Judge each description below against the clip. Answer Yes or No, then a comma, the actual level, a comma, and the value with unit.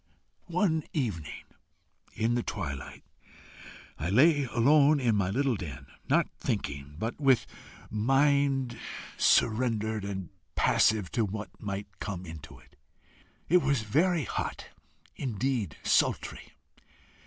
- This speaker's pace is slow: Yes, slow, 110 wpm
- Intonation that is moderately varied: No, wide, 5.7 semitones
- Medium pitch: No, low, 115 Hz